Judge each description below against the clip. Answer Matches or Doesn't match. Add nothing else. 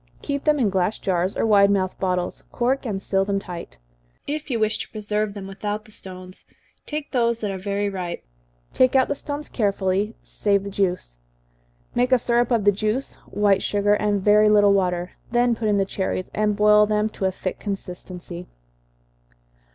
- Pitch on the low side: Doesn't match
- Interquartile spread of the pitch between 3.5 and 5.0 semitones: Doesn't match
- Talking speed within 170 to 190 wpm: Matches